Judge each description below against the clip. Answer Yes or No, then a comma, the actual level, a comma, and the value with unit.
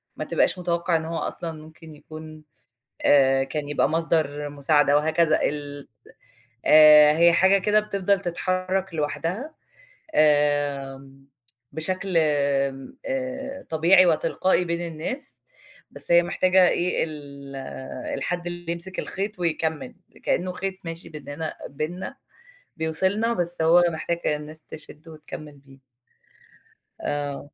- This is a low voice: No, medium, 160 Hz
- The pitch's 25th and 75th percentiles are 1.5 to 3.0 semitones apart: No, average, 3.4 semitones